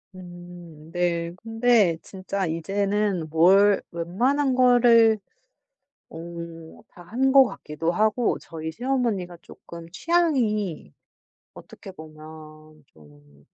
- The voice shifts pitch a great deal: Yes, wide, 5.7 semitones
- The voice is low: No, medium, 185 Hz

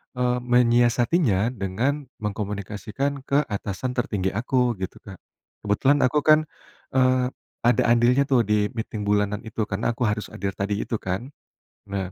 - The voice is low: Yes, low, 115 Hz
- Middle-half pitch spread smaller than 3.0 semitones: No, average, 3.7 semitones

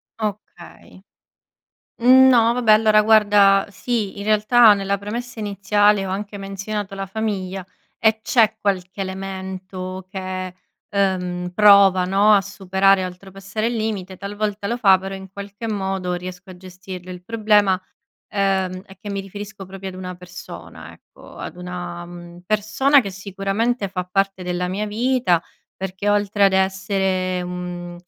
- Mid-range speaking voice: No, high, 195 Hz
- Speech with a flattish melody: Yes, narrow, 2.1 semitones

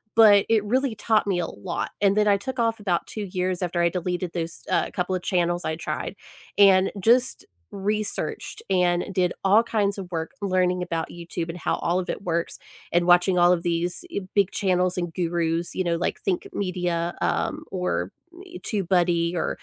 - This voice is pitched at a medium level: Yes, medium, 180 Hz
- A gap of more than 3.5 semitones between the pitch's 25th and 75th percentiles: No, average, 2.7 semitones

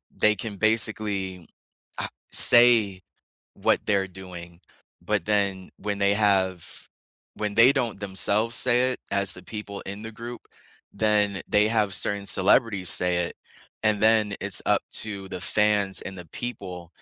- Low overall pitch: Yes, low, 100 Hz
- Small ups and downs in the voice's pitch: Yes, narrow, 2.3 semitones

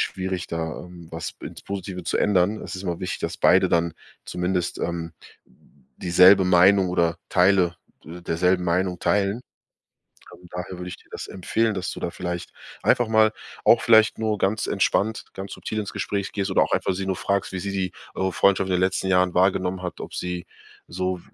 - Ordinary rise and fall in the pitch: No, narrow, 1.8 semitones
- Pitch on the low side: Yes, very low, 95 Hz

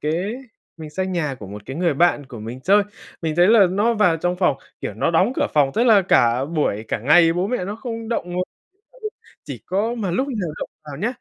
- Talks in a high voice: No, medium, 175 Hz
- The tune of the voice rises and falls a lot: Yes, wide, 5.8 semitones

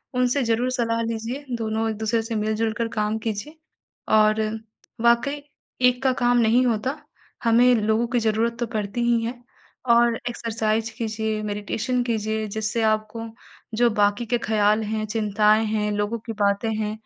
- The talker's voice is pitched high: Yes, high, 225 Hz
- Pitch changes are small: Yes, narrow, 1.7 semitones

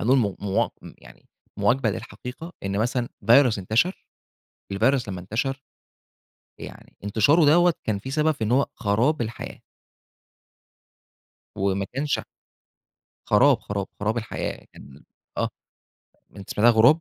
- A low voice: Yes, low, 115 Hz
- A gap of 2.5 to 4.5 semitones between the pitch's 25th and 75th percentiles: No, average, 5.2 semitones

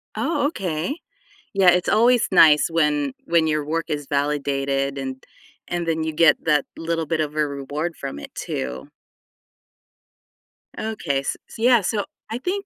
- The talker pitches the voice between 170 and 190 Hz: No, medium, 160 Hz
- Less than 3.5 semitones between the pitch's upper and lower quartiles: No, average, 4.1 semitones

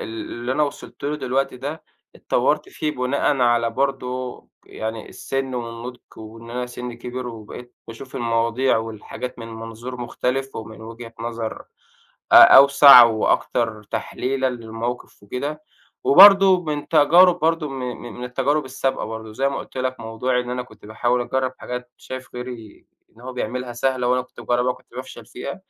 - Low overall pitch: Yes, low, 125 Hz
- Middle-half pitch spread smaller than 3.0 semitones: Yes, narrow, 2.5 semitones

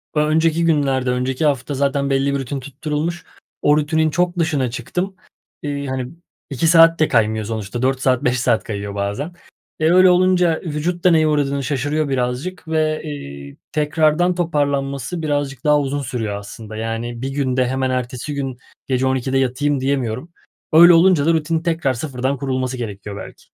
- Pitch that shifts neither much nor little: Yes, average, 3.8 semitones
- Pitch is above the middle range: No, medium, 140 Hz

